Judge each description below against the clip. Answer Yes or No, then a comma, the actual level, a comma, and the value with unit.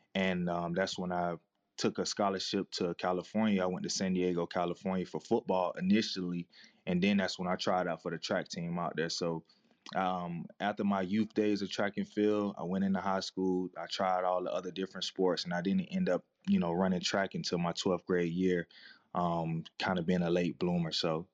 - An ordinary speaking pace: No, fast, 215 wpm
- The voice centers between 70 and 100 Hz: Yes, very low, 90 Hz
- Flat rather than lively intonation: Yes, narrow, 2.3 semitones